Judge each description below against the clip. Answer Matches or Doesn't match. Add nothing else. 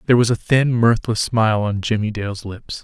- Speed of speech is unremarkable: Doesn't match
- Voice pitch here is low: Matches